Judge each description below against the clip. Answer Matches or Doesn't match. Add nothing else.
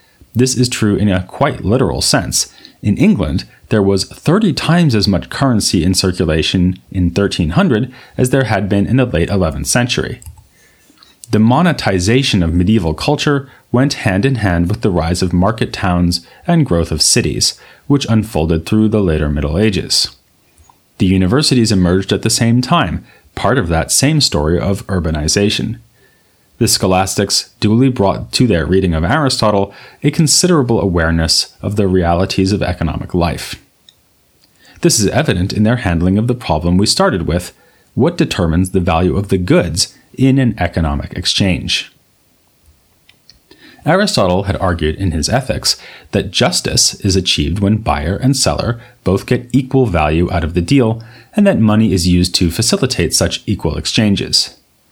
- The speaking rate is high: Doesn't match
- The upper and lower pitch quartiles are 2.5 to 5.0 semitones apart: Doesn't match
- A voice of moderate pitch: Doesn't match